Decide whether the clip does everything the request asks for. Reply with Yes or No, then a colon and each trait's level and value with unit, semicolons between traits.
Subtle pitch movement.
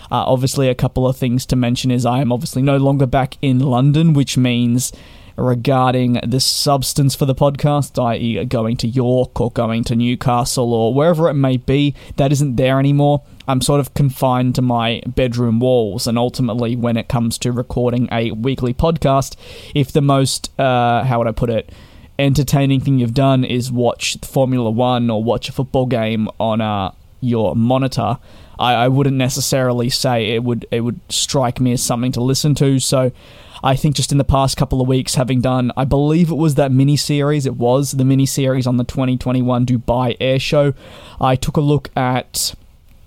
Yes: narrow, 2.2 semitones